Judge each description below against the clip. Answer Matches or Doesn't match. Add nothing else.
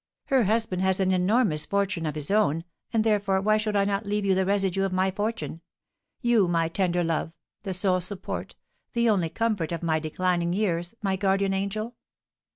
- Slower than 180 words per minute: Doesn't match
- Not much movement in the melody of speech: Doesn't match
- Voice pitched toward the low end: Doesn't match